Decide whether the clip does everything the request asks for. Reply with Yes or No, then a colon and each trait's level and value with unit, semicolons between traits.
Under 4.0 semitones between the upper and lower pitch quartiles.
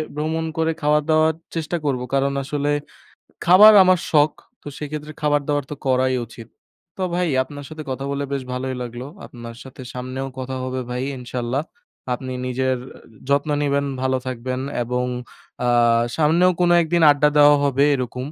Yes: average, 2.9 semitones